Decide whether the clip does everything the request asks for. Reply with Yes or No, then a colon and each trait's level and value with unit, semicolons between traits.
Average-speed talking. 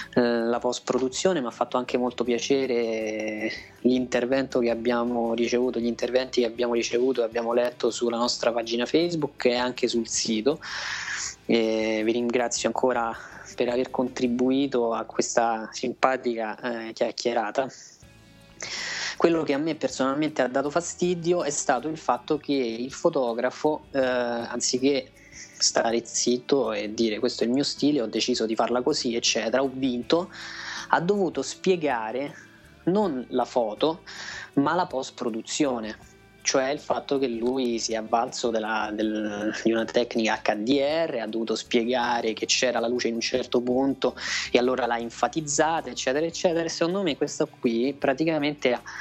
Yes: average, 145 wpm